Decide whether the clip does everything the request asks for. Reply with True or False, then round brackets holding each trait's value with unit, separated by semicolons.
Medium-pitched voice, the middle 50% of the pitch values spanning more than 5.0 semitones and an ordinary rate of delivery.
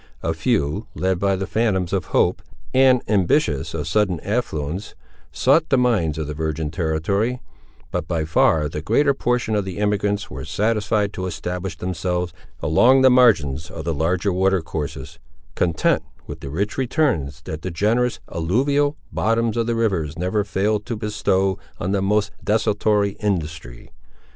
False (95 Hz; 5.4 semitones; 160 wpm)